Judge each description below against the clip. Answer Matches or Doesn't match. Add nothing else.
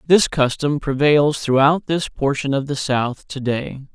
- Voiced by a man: Matches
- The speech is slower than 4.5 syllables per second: Matches